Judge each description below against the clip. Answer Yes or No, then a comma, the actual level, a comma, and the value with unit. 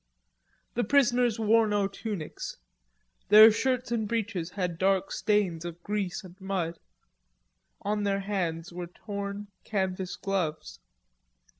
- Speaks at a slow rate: Yes, slow, 120 wpm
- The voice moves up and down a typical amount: Yes, average, 3.2 semitones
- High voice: Yes, high, 200 Hz